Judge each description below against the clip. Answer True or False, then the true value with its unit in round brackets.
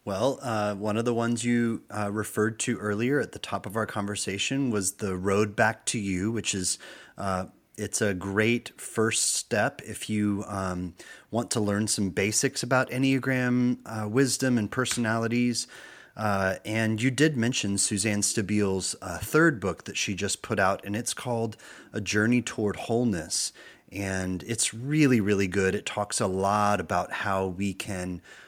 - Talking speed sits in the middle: True (170 wpm)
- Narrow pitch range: False (3.1 semitones)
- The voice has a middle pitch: False (105 Hz)